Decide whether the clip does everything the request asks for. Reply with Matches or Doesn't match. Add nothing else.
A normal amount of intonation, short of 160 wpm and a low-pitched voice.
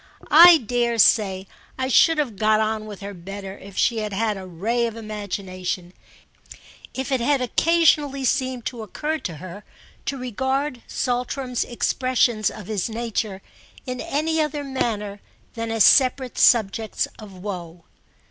Doesn't match